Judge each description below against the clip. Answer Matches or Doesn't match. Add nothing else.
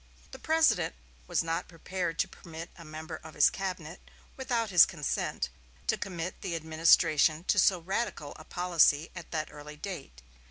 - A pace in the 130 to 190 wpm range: Matches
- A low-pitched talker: Doesn't match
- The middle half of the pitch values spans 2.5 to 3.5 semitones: Matches